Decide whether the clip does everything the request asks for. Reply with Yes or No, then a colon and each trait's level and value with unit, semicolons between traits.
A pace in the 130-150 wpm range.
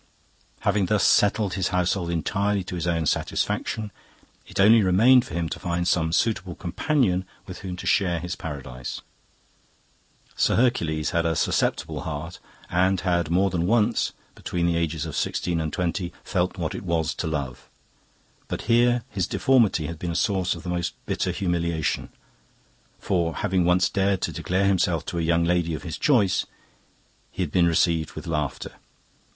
No: average, 170 wpm